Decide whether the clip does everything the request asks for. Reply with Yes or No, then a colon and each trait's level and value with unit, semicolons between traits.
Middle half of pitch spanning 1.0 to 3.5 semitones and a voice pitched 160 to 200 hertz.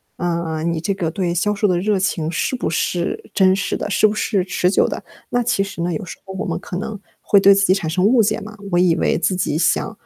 Yes: average, 2.8 semitones; medium, 185 Hz